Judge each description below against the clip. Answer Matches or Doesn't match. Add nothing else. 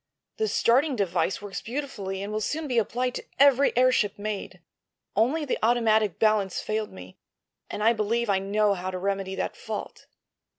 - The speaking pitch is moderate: Doesn't match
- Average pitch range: Matches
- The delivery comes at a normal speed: Matches